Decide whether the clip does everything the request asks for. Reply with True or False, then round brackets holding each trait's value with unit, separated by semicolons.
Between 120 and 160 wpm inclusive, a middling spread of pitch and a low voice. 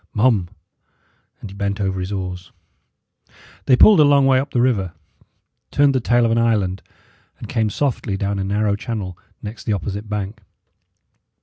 False (170 wpm; 3.8 semitones; 105 Hz)